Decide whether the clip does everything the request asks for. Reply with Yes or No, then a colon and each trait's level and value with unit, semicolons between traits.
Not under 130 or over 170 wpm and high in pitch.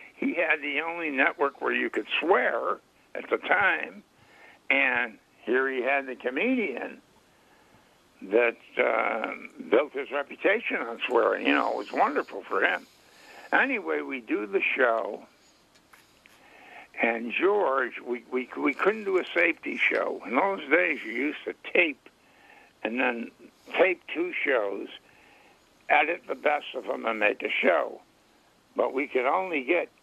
Yes: average, 145 wpm; high, 195 Hz